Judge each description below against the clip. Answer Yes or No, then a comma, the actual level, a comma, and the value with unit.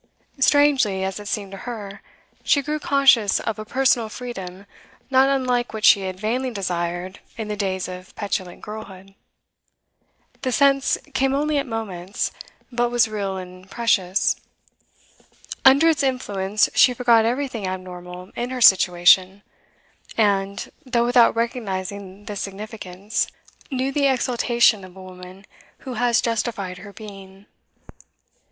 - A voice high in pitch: Yes, high, 215 Hz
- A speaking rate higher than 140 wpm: No, slow, 135 wpm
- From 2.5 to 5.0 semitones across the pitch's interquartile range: Yes, average, 4.6 semitones